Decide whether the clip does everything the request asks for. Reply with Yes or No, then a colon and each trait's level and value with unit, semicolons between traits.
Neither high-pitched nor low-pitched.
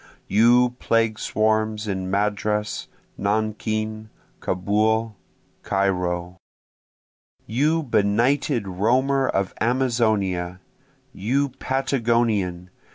No: low, 110 Hz